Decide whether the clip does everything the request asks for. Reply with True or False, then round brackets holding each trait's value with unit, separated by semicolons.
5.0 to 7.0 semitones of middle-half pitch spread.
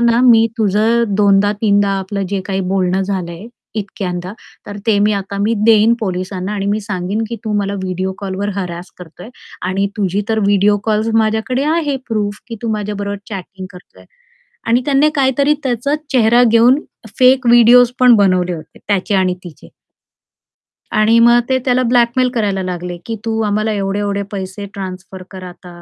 False (3.3 semitones)